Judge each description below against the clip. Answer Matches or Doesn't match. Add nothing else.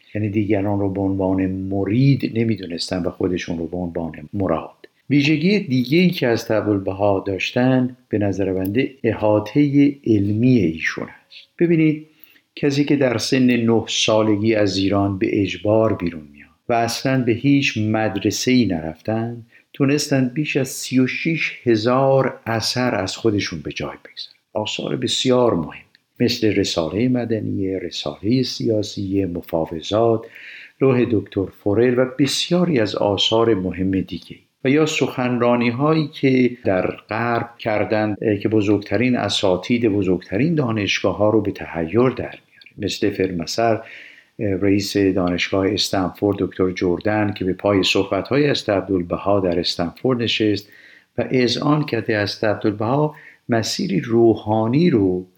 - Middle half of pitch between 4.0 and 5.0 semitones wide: Matches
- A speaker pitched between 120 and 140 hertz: Doesn't match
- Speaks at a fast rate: Doesn't match